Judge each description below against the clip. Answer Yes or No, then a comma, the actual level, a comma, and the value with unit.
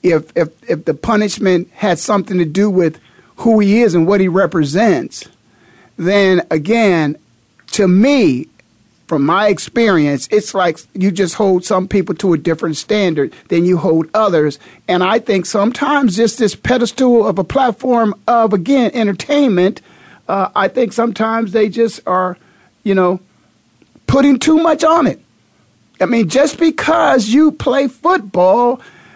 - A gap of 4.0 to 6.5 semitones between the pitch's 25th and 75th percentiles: Yes, average, 4.6 semitones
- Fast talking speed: No, average, 150 wpm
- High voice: Yes, high, 205 Hz